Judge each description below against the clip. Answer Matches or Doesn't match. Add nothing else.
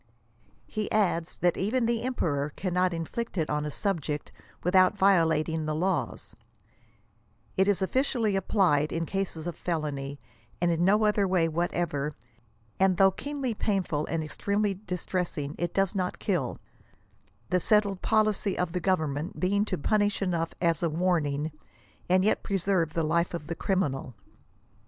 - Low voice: Doesn't match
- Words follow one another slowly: Doesn't match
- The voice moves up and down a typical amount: Matches